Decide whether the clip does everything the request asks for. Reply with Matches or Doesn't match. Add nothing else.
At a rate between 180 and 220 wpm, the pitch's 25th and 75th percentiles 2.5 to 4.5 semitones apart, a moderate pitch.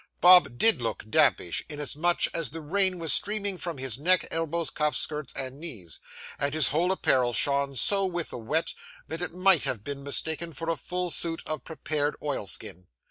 Matches